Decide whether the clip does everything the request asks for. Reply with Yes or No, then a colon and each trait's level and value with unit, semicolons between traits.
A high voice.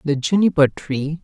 No: medium, 150 Hz